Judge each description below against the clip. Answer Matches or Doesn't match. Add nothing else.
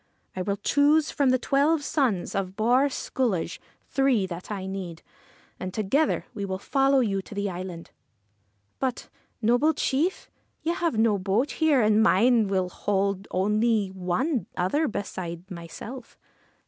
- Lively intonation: Matches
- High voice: Matches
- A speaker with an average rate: Matches